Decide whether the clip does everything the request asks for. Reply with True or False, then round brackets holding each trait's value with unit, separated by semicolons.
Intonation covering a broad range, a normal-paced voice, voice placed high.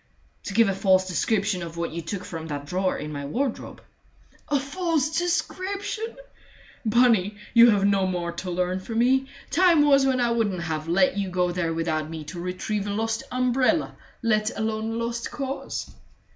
True (5.9 semitones; 180 wpm; 205 Hz)